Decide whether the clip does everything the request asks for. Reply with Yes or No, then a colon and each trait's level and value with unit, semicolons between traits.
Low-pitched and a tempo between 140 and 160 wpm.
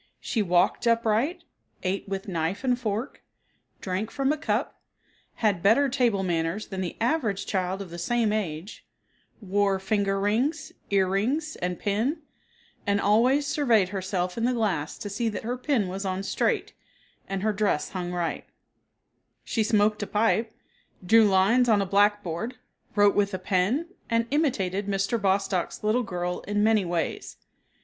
No: high, 205 Hz; average, 155 wpm